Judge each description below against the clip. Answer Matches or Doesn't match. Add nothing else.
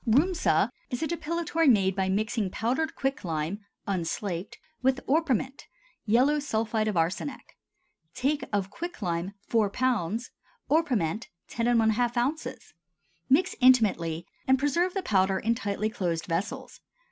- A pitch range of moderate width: Doesn't match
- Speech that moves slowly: Matches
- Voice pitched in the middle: Doesn't match